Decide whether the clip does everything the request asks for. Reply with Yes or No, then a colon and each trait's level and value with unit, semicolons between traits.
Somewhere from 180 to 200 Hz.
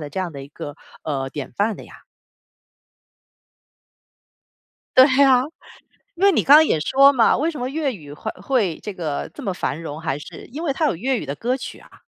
No: high, 210 Hz